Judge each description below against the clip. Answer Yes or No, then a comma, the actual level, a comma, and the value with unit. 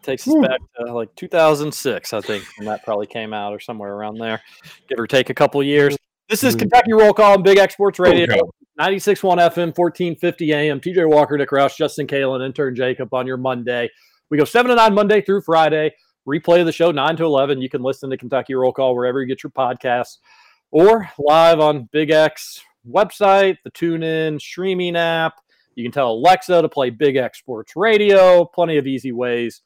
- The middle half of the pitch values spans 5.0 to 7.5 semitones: Yes, wide, 5.6 semitones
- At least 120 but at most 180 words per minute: No, average, 200 wpm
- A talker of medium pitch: Yes, medium, 155 Hz